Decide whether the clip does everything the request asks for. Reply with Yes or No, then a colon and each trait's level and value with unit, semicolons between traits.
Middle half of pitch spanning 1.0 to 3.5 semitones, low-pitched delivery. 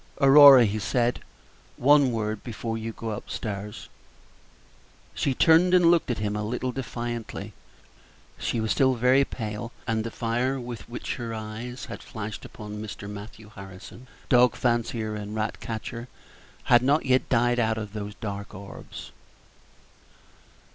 Yes: average, 2.8 semitones; low, 115 Hz